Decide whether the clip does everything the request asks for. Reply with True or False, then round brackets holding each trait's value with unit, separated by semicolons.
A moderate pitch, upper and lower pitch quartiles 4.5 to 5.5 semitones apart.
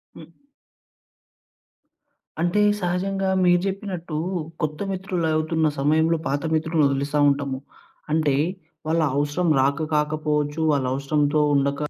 False (155 Hz; 3.1 semitones)